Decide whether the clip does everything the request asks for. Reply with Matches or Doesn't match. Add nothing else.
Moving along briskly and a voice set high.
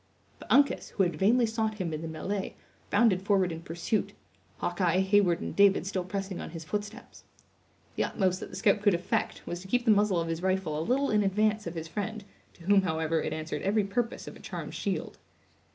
Matches